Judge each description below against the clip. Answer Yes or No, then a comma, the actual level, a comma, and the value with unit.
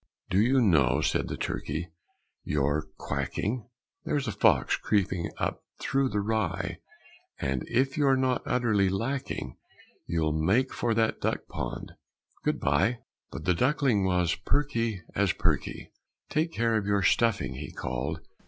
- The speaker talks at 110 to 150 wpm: Yes, average, 145 wpm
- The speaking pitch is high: No, low, 105 Hz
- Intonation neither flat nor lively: No, wide, 6.9 semitones